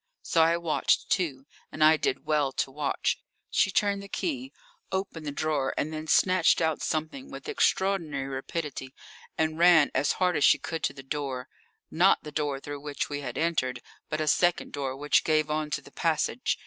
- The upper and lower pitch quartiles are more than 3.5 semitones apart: No, average, 3.1 semitones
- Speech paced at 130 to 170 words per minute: No, average, 190 wpm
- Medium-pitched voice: Yes, medium, 155 Hz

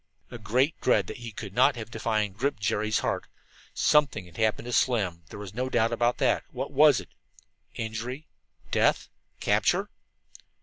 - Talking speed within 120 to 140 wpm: No, average, 165 wpm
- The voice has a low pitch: Yes, low, 115 Hz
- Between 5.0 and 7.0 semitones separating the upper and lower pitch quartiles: No, average, 3.3 semitones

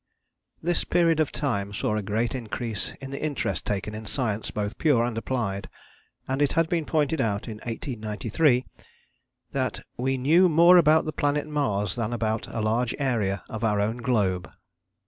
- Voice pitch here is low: Yes, low, 120 Hz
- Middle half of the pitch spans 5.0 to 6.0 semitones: Yes, wide, 5.4 semitones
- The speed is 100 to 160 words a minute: No, average, 170 wpm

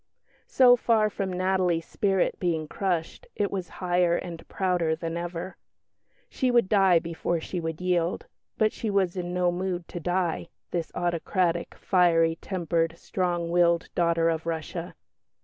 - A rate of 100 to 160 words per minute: Yes, average, 150 wpm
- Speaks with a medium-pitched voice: Yes, medium, 175 Hz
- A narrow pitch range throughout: Yes, narrow, 2.0 semitones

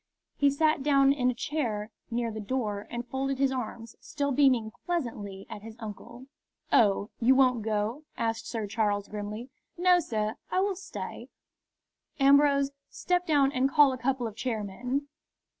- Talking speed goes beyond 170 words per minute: No, average, 160 wpm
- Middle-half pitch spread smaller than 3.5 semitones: No, average, 4.2 semitones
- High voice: Yes, very high, 250 Hz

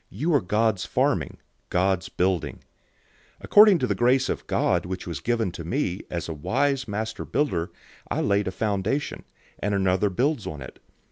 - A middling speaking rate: Yes, average, 175 wpm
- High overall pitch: No, low, 100 Hz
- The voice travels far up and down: Yes, wide, 5.9 semitones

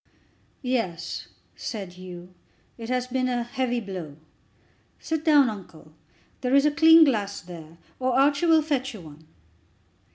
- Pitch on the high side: Yes, high, 245 Hz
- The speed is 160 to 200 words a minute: No, average, 140 wpm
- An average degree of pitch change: No, wide, 7.1 semitones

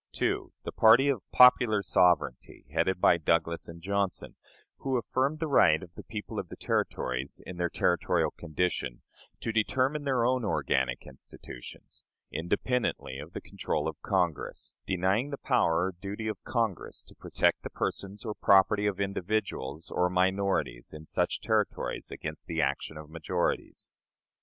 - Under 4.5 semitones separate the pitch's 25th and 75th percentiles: No, average, 5.2 semitones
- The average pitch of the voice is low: Yes, very low, 95 Hz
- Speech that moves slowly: No, average, 150 wpm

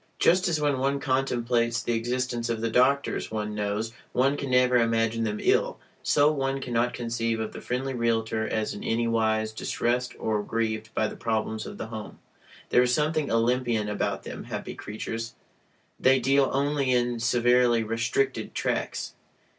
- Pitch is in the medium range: No, low, 120 Hz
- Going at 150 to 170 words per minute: Yes, average, 165 wpm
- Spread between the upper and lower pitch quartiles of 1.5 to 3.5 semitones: Yes, narrow, 2.4 semitones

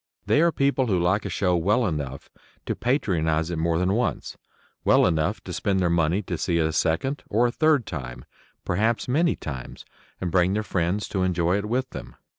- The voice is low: Yes, very low, 90 Hz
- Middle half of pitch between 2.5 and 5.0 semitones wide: No, wide, 5.4 semitones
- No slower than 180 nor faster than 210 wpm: Yes, fast, 205 wpm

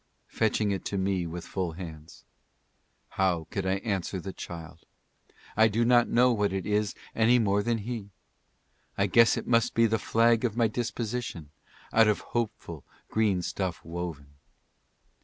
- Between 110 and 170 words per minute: Yes, average, 160 wpm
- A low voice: Yes, low, 100 Hz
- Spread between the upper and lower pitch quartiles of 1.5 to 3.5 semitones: No, average, 4.4 semitones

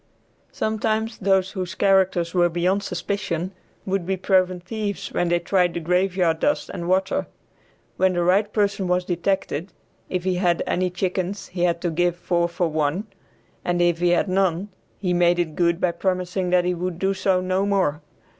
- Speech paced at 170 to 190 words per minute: Yes, average, 180 wpm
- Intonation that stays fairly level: Yes, narrow, 1.7 semitones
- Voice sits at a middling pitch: Yes, medium, 180 Hz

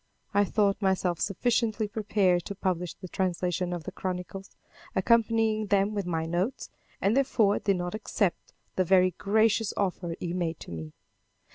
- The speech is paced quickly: No, average, 155 wpm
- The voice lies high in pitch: Yes, high, 195 Hz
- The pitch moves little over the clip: No, average, 3.1 semitones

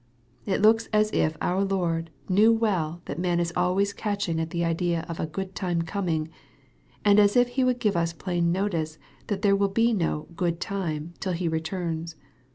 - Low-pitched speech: No, medium, 180 Hz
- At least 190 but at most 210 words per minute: Yes, average, 200 wpm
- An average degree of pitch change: Yes, average, 3.3 semitones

